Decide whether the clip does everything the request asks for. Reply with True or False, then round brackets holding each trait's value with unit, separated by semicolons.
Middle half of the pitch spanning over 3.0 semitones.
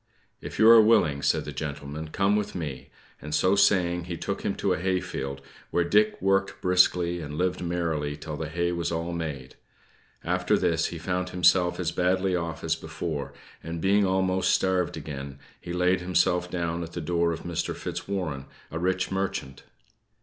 False (2.5 semitones)